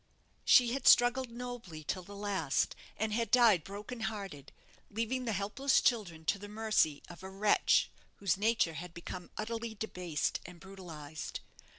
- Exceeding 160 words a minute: No, average, 155 wpm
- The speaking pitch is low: No, high, 205 Hz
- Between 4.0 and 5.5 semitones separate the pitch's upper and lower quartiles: Yes, average, 4.6 semitones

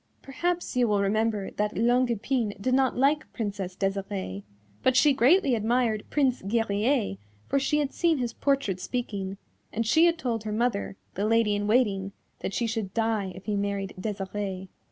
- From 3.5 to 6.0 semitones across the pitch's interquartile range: Yes, average, 4.2 semitones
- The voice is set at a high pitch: Yes, high, 220 Hz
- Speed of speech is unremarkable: Yes, average, 175 wpm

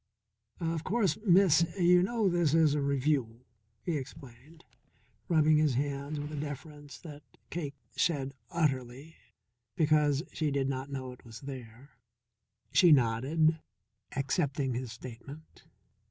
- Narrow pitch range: No, average, 3.3 semitones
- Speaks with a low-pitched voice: No, medium, 145 Hz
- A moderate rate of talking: No, slow, 125 wpm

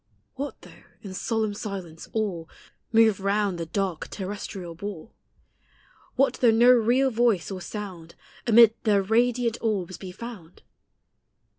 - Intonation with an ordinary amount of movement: Yes, average, 3.7 semitones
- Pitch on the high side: Yes, high, 210 Hz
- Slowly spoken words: Yes, slow, 130 wpm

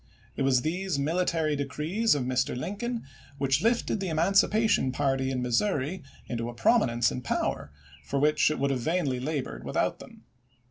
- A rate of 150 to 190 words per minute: Yes, average, 165 wpm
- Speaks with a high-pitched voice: No, medium, 145 Hz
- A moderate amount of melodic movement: No, wide, 5.9 semitones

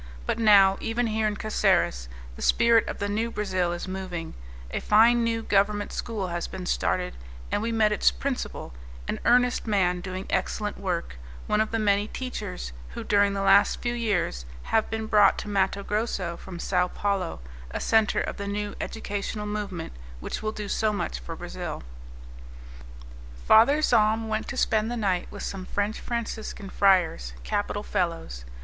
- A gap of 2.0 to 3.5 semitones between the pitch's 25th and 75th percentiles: Yes, average, 2.8 semitones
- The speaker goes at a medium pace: Yes, average, 170 wpm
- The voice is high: Yes, high, 205 Hz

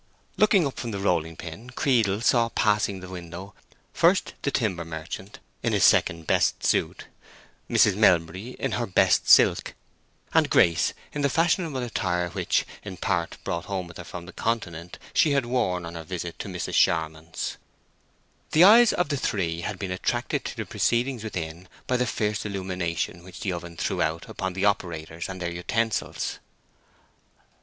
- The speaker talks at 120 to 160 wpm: No, average, 170 wpm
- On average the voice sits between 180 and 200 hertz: No, very low, 95 Hz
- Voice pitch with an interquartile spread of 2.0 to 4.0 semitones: No, wide, 5.4 semitones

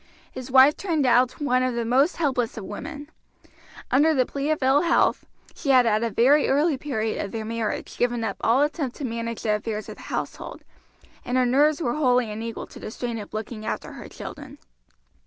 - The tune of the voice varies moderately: Yes, average, 3.9 semitones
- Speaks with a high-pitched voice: Yes, very high, 250 Hz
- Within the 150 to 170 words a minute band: No, fast, 205 wpm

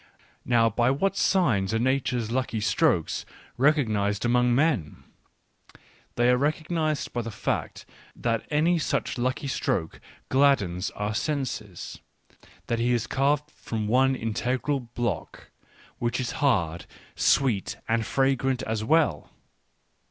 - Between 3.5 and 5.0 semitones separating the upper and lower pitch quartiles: Yes, average, 3.8 semitones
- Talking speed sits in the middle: No, slow, 120 wpm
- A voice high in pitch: No, low, 125 Hz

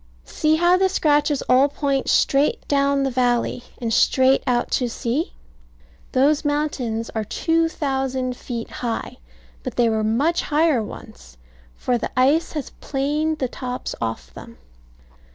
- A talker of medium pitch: No, very high, 270 Hz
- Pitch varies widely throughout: No, average, 3.7 semitones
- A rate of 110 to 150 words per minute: Yes, average, 140 wpm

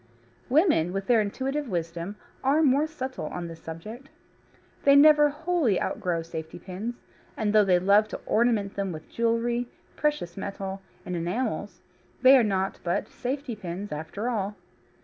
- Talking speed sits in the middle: Yes, average, 150 wpm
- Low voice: No, high, 210 Hz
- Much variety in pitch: Yes, wide, 6.3 semitones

